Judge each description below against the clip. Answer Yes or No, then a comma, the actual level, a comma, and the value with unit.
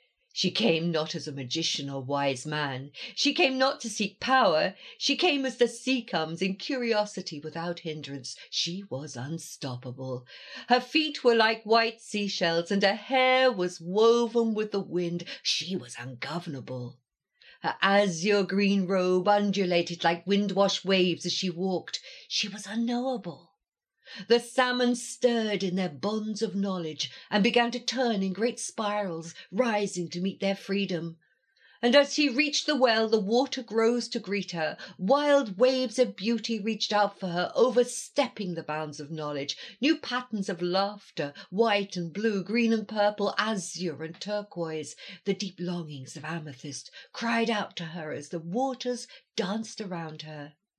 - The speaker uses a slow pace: No, average, 155 wpm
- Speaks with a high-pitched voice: Yes, high, 200 Hz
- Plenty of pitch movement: Yes, wide, 5.7 semitones